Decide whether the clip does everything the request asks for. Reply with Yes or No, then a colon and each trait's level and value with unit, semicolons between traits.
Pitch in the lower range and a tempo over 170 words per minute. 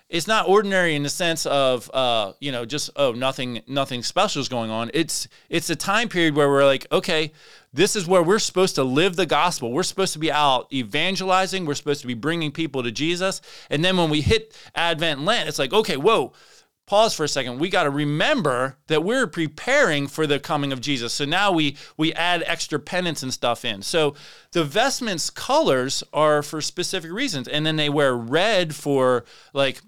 No: medium, 150 Hz; fast, 205 wpm